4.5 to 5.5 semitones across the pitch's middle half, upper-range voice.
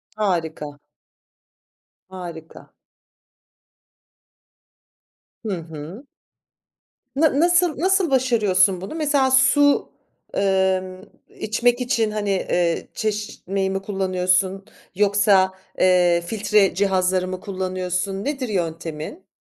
No: average, 4.0 semitones; high, 195 Hz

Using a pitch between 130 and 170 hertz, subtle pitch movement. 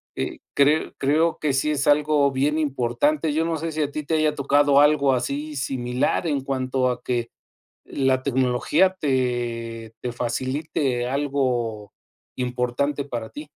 No: medium, 140 Hz; average, 3.1 semitones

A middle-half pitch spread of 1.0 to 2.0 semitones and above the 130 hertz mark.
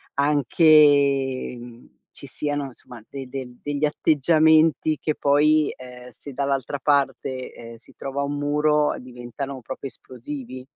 No: narrow, 2.4 semitones; medium, 140 Hz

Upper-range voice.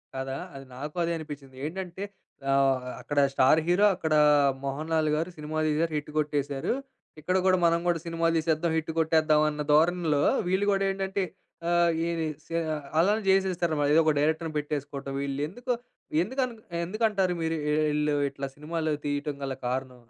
No: medium, 155 Hz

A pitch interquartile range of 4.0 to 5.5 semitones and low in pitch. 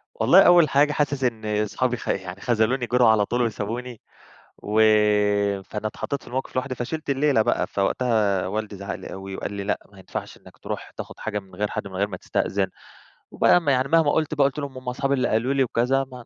Yes: average, 4.6 semitones; low, 115 Hz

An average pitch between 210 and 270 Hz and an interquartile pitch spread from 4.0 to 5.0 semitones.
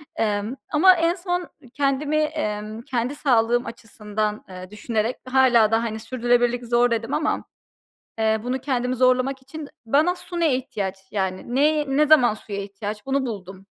Yes: high, 245 Hz; average, 4.3 semitones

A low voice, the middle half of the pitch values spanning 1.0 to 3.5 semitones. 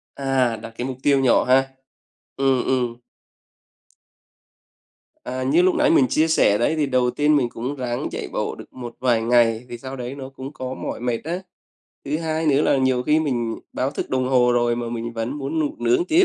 Yes: low, 130 Hz; average, 2.7 semitones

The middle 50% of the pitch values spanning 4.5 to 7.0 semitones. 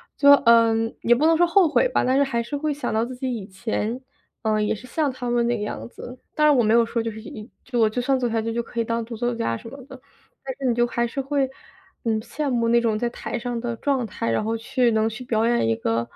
No: narrow, 2.5 semitones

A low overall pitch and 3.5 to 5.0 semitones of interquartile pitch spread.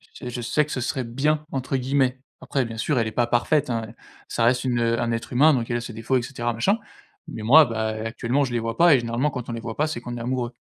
No: low, 120 Hz; narrow, 2.6 semitones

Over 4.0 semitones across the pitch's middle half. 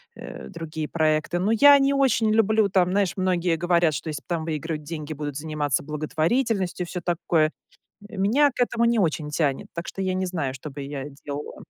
Yes: average, 4.5 semitones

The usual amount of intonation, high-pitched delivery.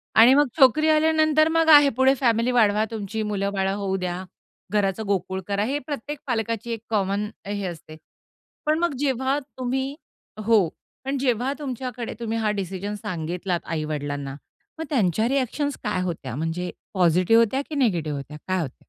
No: wide, 6.2 semitones; high, 220 Hz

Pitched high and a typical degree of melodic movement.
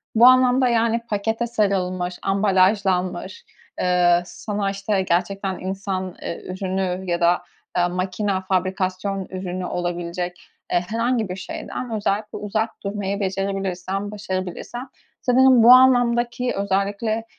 Yes: high, 195 Hz; average, 3.2 semitones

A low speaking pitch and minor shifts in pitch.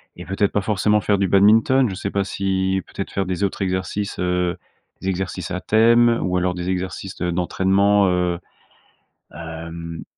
Yes: very low, 95 Hz; narrow, 1.9 semitones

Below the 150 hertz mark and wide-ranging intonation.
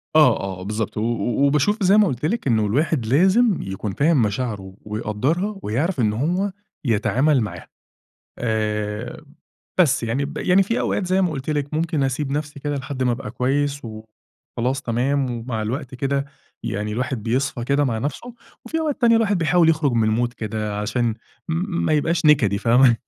Yes: low, 135 Hz; wide, 5.7 semitones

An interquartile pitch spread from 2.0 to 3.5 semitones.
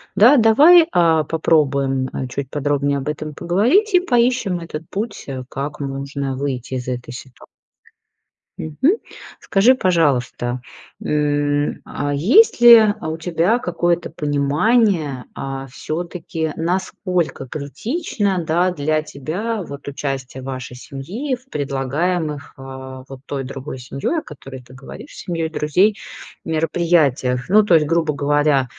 No: average, 5.0 semitones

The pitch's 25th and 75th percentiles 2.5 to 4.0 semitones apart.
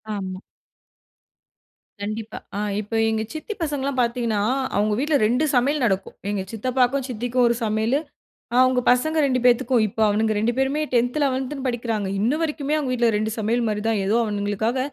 Yes: average, 3.4 semitones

